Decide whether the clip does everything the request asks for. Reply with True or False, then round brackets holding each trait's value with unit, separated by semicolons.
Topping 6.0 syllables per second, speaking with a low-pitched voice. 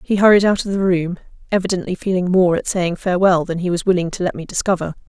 False (6.6 syllables/s; 180 Hz)